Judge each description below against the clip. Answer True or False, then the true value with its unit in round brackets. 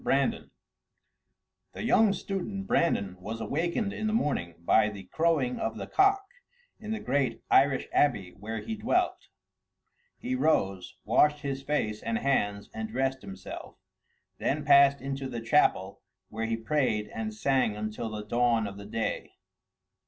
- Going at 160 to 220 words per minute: False (150 wpm)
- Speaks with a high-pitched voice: False (130 Hz)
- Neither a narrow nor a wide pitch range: False (6.7 semitones)